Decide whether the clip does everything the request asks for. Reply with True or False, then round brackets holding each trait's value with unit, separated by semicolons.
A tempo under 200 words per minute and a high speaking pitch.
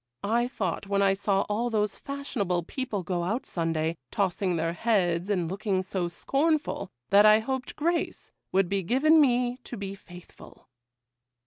True (155 wpm; 200 Hz)